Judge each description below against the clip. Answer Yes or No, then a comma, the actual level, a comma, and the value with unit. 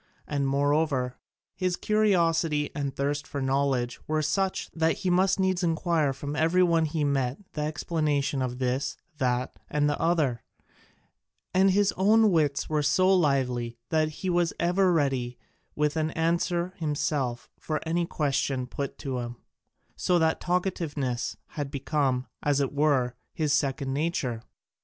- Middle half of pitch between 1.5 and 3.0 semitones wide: No, average, 3.8 semitones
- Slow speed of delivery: No, average, 145 wpm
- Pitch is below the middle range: No, medium, 150 Hz